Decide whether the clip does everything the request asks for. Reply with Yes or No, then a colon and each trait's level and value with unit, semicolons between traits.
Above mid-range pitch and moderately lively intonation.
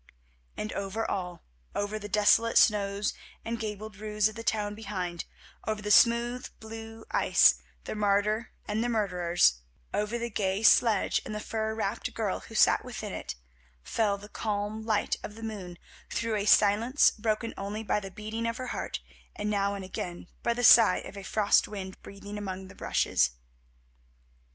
No: high, 210 Hz; narrow, 1.9 semitones